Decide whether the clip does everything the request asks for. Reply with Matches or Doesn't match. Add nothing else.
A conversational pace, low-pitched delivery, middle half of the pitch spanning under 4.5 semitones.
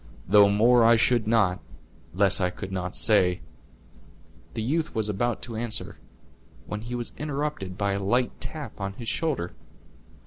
Matches